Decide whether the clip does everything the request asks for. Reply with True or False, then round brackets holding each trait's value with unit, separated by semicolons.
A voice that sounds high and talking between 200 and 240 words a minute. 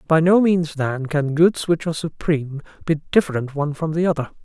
False (155 Hz; 205 wpm)